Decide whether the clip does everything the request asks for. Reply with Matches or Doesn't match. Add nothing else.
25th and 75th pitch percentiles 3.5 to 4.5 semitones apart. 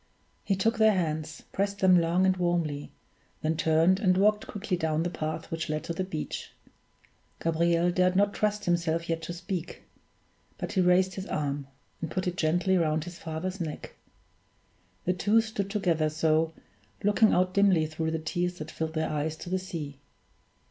Doesn't match